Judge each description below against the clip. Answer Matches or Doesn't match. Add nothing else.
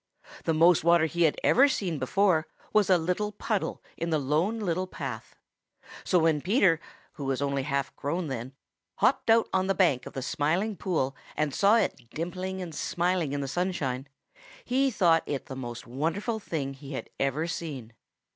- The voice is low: Doesn't match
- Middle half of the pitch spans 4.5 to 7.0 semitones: Matches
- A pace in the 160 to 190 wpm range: Matches